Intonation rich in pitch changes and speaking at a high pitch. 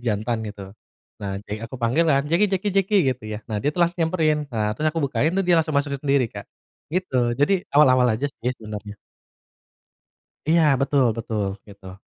No: wide, 6.7 semitones; low, 135 Hz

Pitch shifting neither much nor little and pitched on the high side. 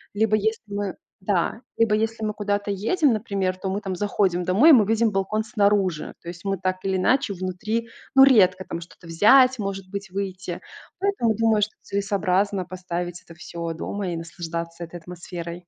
Yes: average, 3.1 semitones; high, 195 Hz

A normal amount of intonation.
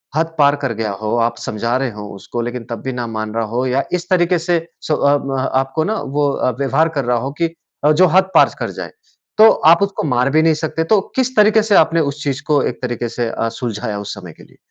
No: wide, 5.7 semitones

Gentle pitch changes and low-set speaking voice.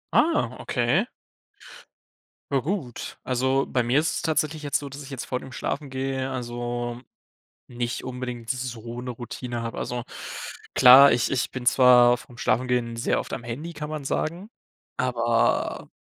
Yes: narrow, 2.3 semitones; low, 125 Hz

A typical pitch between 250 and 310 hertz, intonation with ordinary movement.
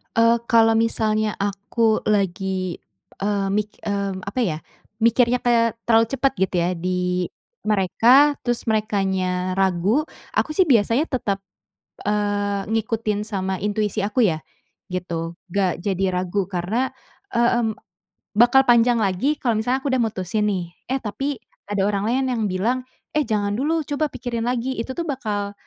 No: high, 215 Hz; average, 3.6 semitones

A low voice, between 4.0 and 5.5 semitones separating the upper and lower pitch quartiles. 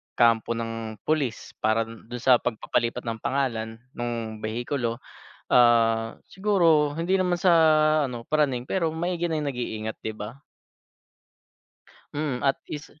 Yes: low, 120 Hz; average, 5.0 semitones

